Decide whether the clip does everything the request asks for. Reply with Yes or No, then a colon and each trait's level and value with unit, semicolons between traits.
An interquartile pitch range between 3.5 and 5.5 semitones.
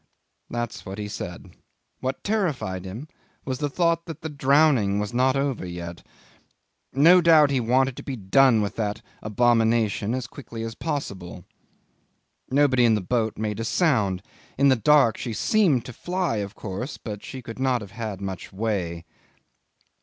Yes: average, 5.1 semitones